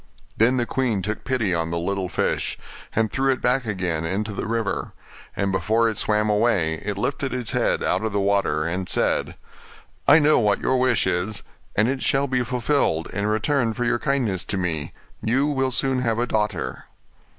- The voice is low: Yes, low, 110 Hz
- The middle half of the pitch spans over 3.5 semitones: Yes, average, 4.7 semitones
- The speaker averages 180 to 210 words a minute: Yes, average, 195 wpm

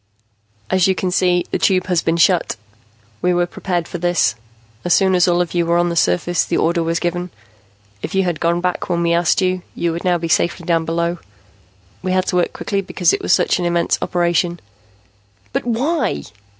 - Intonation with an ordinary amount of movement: No, narrow, 1.3 semitones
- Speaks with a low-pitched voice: No, medium, 175 Hz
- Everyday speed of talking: No, fast, 210 wpm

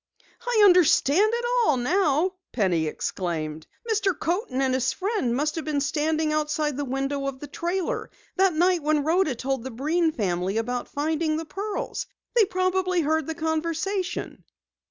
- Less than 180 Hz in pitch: No, very high, 310 Hz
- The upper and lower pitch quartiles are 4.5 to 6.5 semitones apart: Yes, average, 5.3 semitones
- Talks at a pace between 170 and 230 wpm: No, average, 155 wpm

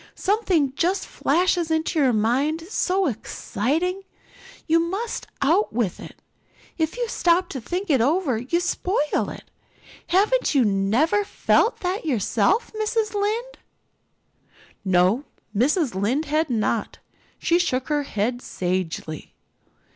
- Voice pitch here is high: Yes, very high, 315 Hz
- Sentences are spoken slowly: Yes, slow, 130 wpm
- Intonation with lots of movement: Yes, wide, 7.5 semitones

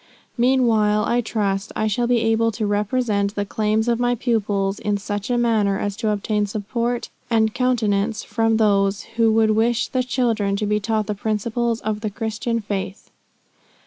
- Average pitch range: No, narrow, 2.2 semitones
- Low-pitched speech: No, high, 220 Hz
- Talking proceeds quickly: No, average, 175 wpm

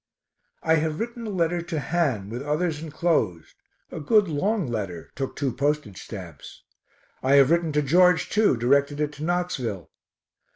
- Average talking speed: Yes, average, 160 wpm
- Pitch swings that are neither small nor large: Yes, average, 4.9 semitones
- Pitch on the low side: No, medium, 150 Hz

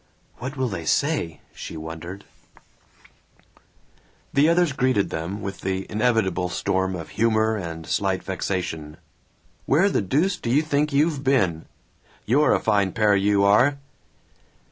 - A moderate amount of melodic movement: No, wide, 6.6 semitones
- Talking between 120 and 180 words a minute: Yes, slow, 135 wpm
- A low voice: Yes, low, 105 Hz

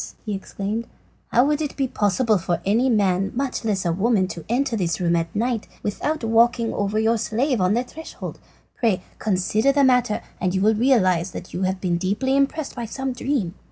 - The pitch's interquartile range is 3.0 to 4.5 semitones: No, average, 5.0 semitones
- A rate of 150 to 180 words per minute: No, average, 195 wpm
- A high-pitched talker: Yes, high, 220 Hz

